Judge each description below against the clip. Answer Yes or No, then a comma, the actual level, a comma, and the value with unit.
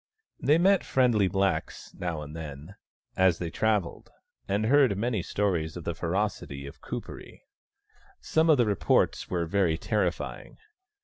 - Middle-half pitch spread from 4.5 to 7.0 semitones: Yes, average, 4.8 semitones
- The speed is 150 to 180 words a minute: No, average, 140 wpm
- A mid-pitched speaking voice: No, very low, 95 Hz